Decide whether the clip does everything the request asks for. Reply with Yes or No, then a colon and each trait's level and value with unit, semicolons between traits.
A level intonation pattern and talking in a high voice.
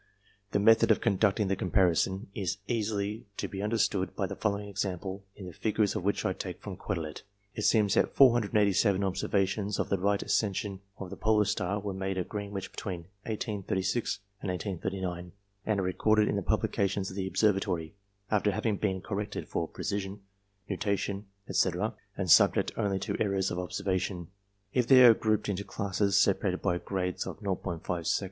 No: narrow, 1.9 semitones; low, 100 Hz